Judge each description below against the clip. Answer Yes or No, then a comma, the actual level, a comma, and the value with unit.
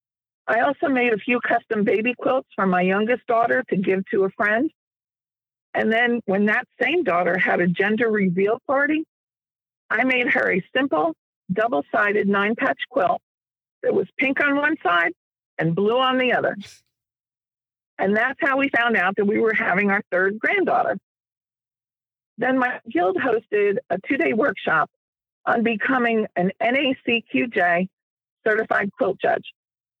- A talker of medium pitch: No, high, 225 Hz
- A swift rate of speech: No, average, 155 wpm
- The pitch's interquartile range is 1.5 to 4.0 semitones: No, average, 5.3 semitones